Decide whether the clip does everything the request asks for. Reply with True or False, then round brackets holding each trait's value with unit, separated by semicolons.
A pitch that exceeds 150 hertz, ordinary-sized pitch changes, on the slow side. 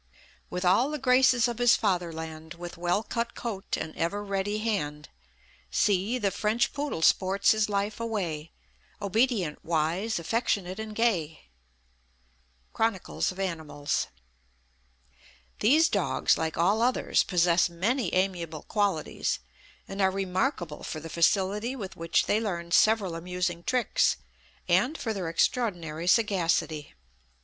True (190 Hz; 4.6 semitones; 125 wpm)